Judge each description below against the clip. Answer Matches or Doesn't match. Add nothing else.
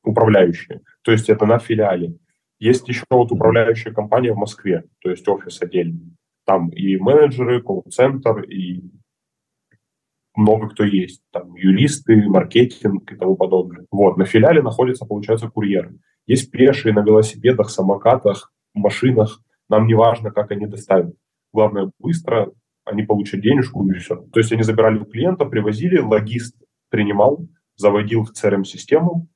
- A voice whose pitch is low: Matches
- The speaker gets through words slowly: Doesn't match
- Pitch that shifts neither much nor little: Matches